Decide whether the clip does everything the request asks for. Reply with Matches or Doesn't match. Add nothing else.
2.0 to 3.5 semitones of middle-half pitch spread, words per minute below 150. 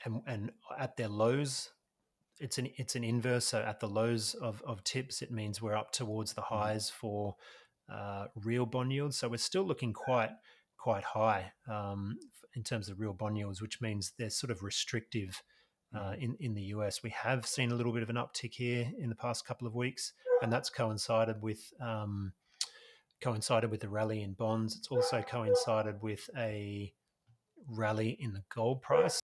Doesn't match